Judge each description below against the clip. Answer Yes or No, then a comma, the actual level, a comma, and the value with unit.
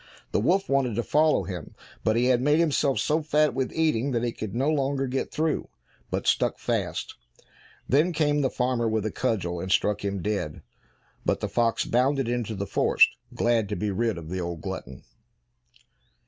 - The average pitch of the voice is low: Yes, low, 120 Hz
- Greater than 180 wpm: Yes, average, 190 wpm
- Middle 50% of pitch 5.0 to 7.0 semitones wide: Yes, average, 5.3 semitones